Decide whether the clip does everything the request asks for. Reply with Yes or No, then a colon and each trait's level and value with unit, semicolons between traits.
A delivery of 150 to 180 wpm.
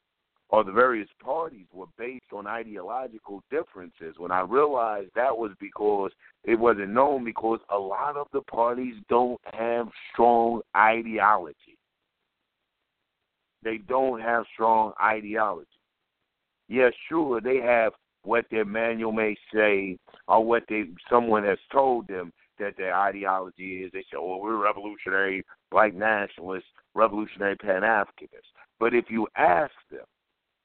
No: slow, 135 wpm